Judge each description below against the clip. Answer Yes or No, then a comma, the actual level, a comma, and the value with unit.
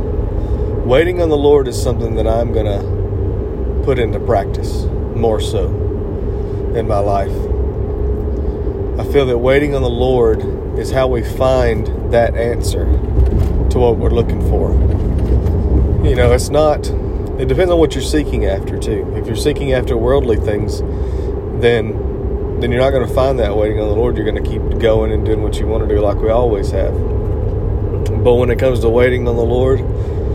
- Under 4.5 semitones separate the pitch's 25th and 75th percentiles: Yes, average, 3.1 semitones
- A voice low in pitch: Yes, low, 105 Hz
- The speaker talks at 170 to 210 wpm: Yes, average, 180 wpm